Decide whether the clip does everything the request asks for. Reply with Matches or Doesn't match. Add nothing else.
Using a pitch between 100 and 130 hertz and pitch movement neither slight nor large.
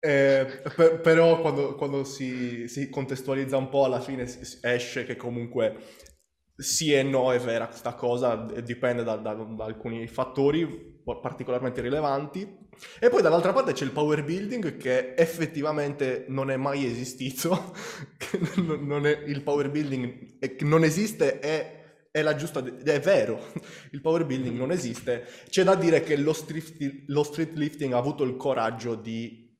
Doesn't match